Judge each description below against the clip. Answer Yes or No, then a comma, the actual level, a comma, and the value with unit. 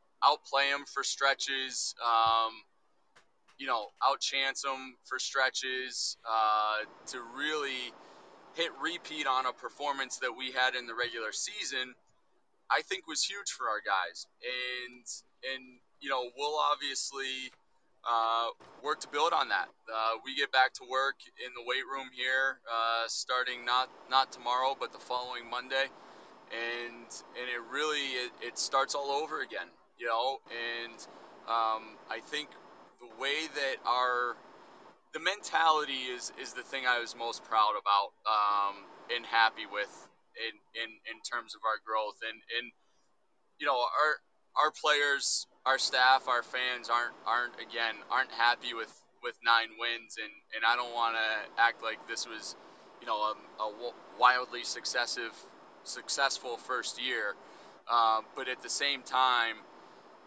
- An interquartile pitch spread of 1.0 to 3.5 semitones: Yes, narrow, 2.5 semitones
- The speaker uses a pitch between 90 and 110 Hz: No, low, 125 Hz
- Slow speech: No, average, 150 wpm